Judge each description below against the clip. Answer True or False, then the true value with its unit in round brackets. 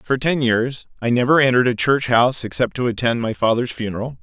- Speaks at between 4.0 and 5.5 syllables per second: False (5.9 syllables/s)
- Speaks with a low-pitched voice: True (120 Hz)